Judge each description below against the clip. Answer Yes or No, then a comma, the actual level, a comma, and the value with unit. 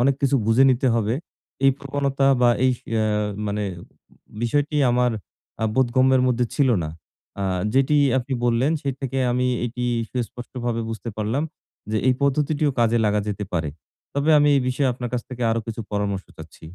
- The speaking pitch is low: Yes, low, 125 Hz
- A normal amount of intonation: Yes, average, 3.1 semitones